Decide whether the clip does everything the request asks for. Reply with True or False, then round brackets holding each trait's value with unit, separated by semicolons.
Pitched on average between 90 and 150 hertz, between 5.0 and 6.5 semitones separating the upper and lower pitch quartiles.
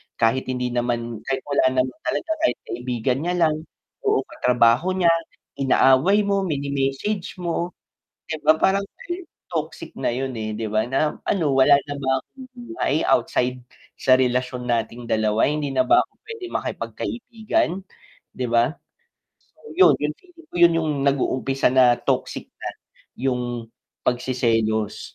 True (135 Hz; 5.6 semitones)